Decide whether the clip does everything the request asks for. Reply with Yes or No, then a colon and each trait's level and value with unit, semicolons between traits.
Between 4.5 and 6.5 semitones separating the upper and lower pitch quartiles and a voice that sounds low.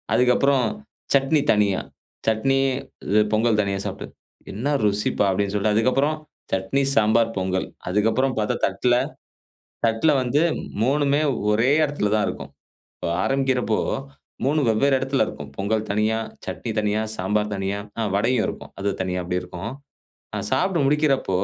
Yes: average, 4.8 semitones; low, 110 Hz